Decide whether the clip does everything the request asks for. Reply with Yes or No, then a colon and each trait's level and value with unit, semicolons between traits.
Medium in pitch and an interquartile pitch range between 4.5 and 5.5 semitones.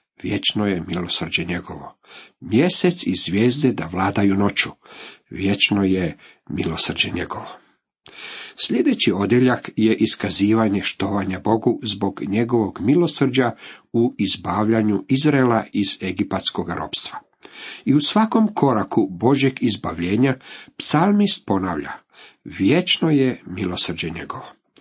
No: low, 110 Hz; average, 5.2 semitones